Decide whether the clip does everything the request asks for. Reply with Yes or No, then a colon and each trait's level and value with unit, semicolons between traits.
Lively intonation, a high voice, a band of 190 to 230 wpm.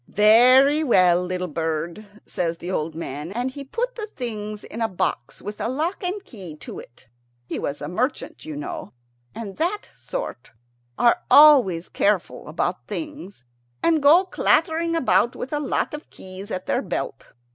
No: wide, 8.9 semitones; high, 230 Hz; average, 170 wpm